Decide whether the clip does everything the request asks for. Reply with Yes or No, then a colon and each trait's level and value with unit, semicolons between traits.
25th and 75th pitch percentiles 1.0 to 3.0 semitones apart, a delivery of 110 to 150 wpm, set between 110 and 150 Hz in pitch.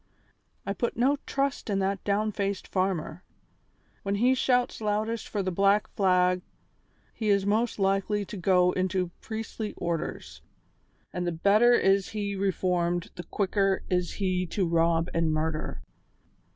No: narrow, 2.6 semitones; average, 140 wpm; high, 195 Hz